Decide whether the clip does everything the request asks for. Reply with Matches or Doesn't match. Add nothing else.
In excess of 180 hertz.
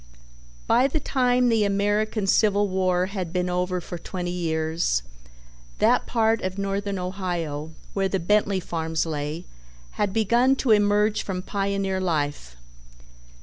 Matches